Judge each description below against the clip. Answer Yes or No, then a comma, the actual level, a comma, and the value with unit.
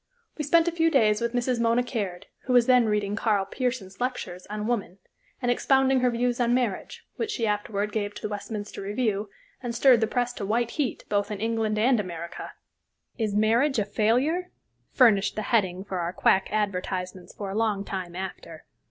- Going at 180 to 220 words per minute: Yes, average, 190 wpm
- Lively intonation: No, average, 3.6 semitones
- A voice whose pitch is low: No, high, 220 Hz